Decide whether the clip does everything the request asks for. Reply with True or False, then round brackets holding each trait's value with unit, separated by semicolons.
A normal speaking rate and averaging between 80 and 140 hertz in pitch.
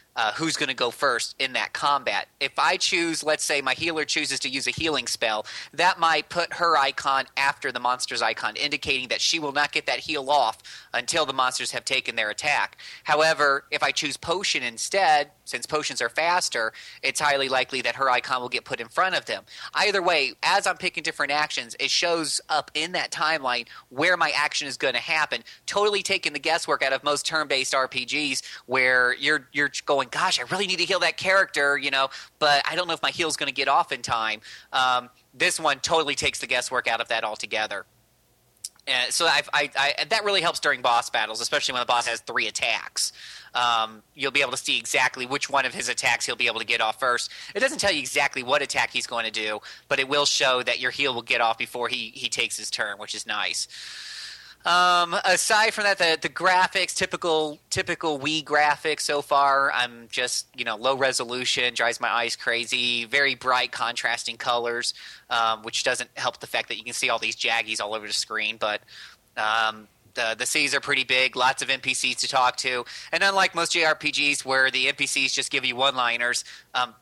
False (215 wpm; 135 Hz)